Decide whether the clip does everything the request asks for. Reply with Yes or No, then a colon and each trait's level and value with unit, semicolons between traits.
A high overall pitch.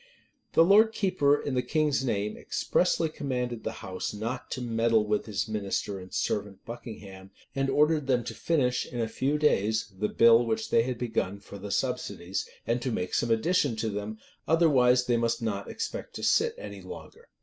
No: low, 120 Hz